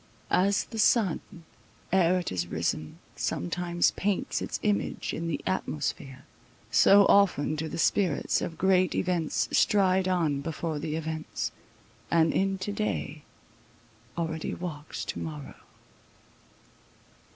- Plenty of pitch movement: No, average, 3.7 semitones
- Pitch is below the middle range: No, medium, 170 Hz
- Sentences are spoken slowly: Yes, slow, 120 wpm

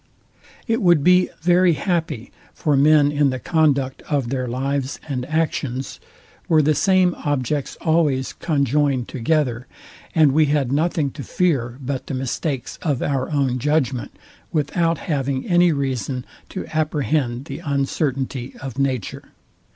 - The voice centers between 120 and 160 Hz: Yes, medium, 140 Hz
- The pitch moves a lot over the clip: No, average, 3.2 semitones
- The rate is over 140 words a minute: No, slow, 135 wpm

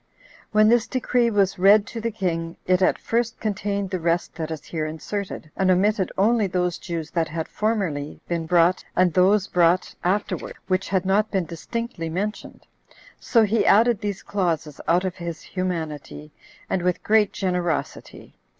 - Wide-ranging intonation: No, average, 3.6 semitones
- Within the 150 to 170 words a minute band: Yes, average, 165 wpm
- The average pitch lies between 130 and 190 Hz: Yes, medium, 185 Hz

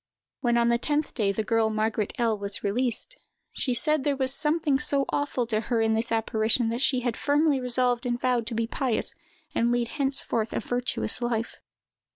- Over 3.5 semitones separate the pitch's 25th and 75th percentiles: No, average, 2.9 semitones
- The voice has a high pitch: Yes, high, 240 Hz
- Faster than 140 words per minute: Yes, average, 200 wpm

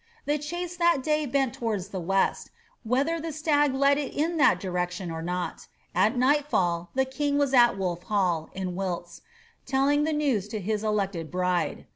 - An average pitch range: No, wide, 8.0 semitones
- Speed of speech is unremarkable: Yes, average, 175 wpm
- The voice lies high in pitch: Yes, high, 235 Hz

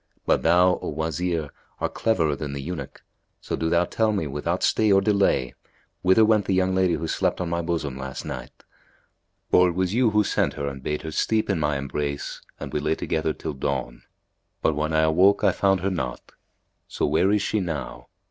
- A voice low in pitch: Yes, very low, 85 Hz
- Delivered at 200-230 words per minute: Yes, fast, 205 wpm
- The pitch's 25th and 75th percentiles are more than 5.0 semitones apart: No, average, 4.4 semitones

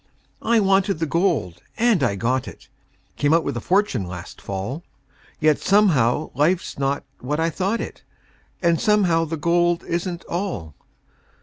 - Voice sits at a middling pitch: Yes, medium, 165 Hz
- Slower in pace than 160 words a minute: Yes, average, 150 wpm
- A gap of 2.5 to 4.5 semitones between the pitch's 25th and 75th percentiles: No, wide, 5.6 semitones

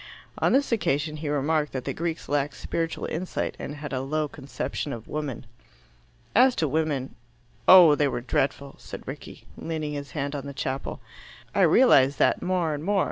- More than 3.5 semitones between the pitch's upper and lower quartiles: No, average, 2.7 semitones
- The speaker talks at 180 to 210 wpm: Yes, average, 185 wpm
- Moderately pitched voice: Yes, medium, 150 Hz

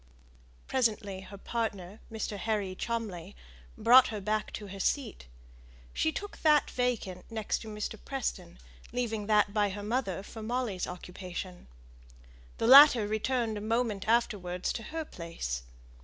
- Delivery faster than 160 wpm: No, average, 140 wpm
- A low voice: No, high, 215 Hz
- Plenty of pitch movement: No, average, 3.6 semitones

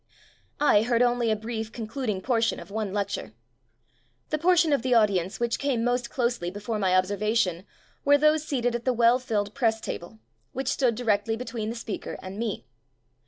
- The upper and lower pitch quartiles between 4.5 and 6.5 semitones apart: No, average, 3.1 semitones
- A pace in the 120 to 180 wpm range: No, average, 190 wpm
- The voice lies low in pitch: No, high, 230 Hz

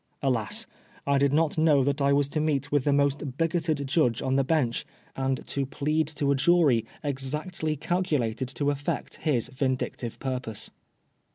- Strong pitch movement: No, narrow, 2.6 semitones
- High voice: No, medium, 140 Hz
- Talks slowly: No, average, 170 wpm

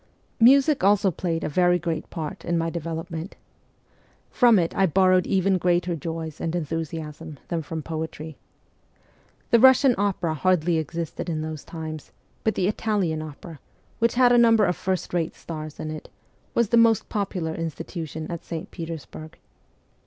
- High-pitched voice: No, medium, 170 Hz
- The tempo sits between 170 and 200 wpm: No, average, 160 wpm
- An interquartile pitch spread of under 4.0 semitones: Yes, average, 3.4 semitones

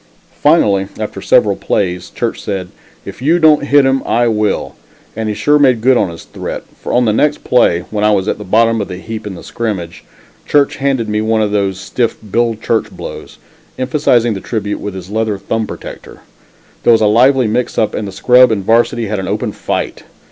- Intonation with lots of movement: No, average, 3.4 semitones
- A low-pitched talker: Yes, low, 110 Hz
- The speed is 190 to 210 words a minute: Yes, fast, 205 wpm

